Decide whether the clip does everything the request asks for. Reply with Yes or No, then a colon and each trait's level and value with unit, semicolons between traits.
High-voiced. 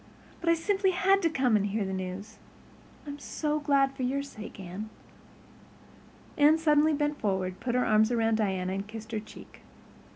Yes: high, 240 Hz